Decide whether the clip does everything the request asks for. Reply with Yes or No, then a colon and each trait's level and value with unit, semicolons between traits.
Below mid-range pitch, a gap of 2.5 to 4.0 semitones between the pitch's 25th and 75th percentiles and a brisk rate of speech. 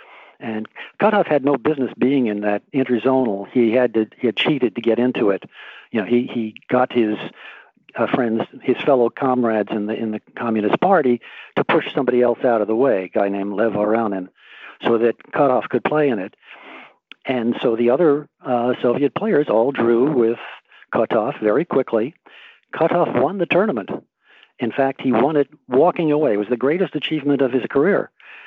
No: low, 120 Hz; average, 3.2 semitones; average, 185 wpm